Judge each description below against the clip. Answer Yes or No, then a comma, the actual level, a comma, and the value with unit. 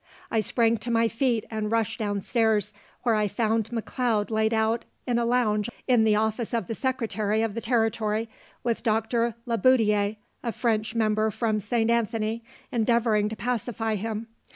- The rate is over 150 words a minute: Yes, average, 170 wpm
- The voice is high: Yes, high, 225 Hz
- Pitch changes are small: Yes, narrow, 1.5 semitones